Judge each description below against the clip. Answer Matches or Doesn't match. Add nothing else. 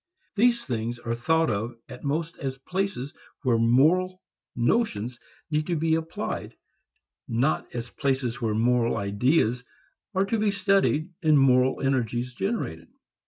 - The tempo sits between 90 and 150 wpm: Matches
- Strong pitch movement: Matches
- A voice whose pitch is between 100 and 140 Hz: Matches